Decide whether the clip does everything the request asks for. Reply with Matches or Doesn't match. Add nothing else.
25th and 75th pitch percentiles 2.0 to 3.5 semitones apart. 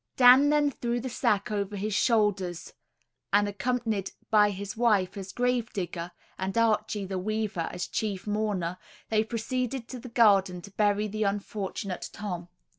Matches